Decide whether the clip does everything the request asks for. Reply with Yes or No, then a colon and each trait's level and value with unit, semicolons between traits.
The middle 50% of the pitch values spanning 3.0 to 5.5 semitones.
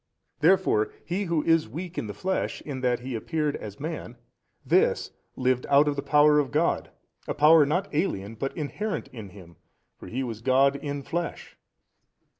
Yes: average, 4.8 semitones